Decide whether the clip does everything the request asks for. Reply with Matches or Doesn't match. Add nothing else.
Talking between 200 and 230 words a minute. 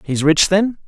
Doesn't match